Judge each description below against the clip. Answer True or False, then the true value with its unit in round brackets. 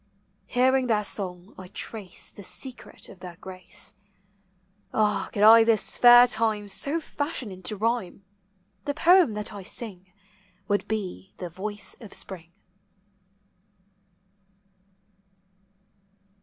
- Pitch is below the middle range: False (210 Hz)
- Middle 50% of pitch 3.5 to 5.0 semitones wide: True (3.8 semitones)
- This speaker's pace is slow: True (120 wpm)